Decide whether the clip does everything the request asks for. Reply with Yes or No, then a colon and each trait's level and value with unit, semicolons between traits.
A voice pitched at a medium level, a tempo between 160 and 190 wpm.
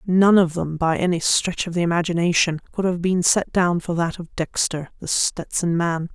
No: medium, 175 Hz; fast, 205 wpm